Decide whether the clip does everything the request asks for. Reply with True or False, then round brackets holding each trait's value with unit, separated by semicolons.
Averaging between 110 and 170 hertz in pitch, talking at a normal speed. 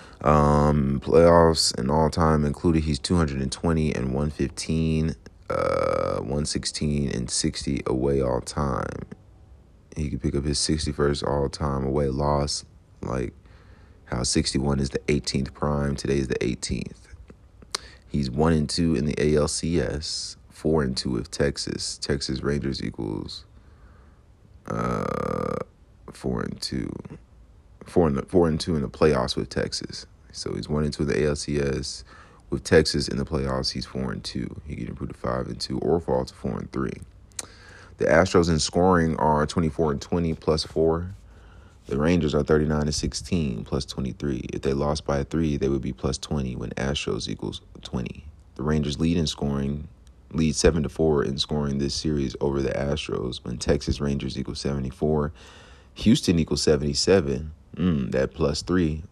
False (75 Hz; 170 wpm)